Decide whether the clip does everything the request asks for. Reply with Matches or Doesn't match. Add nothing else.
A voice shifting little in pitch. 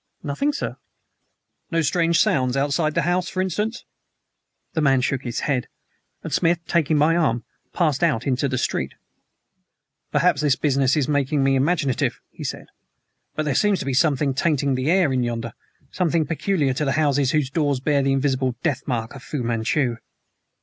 Doesn't match